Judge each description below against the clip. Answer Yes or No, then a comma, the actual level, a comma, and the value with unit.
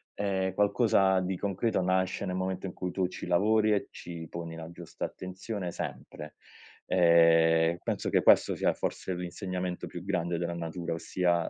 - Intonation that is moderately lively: No, narrow, 1.9 semitones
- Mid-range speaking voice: No, very low, 90 Hz